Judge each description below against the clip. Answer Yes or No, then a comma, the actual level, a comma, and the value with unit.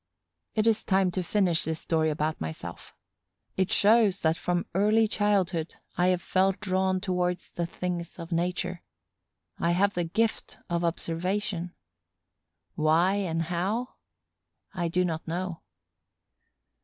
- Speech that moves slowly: Yes, slow, 130 wpm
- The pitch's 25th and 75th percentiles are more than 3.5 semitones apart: No, narrow, 2.4 semitones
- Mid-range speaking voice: Yes, medium, 180 Hz